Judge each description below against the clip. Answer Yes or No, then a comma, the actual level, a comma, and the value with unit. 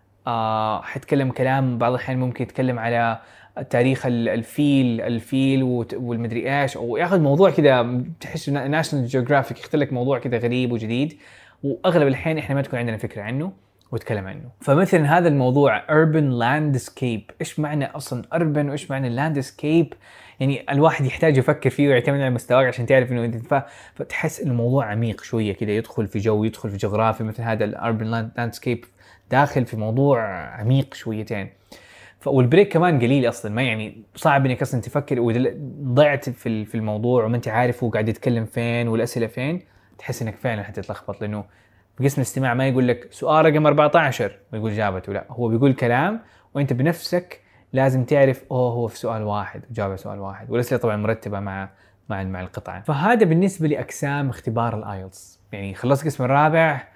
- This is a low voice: Yes, low, 125 Hz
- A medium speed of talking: No, fast, 155 wpm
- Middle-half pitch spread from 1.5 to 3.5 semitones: No, average, 3.9 semitones